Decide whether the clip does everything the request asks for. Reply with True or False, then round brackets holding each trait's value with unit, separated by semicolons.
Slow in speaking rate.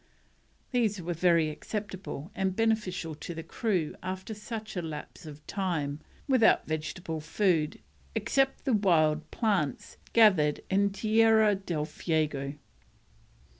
True (120 wpm)